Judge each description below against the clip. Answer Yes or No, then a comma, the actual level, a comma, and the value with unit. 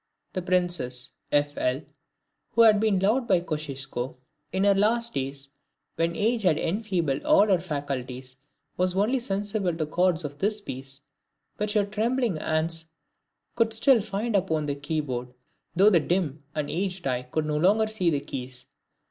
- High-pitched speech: No, medium, 175 Hz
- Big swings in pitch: Yes, wide, 6.3 semitones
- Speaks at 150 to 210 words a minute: Yes, average, 165 wpm